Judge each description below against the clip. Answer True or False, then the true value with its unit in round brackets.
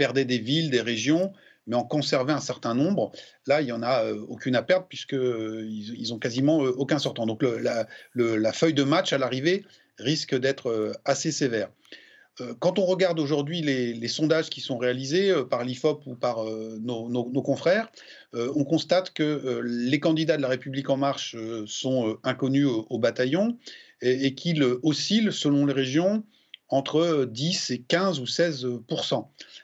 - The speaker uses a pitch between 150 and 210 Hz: False (135 Hz)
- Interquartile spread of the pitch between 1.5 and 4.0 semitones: False (4.4 semitones)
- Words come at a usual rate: True (195 wpm)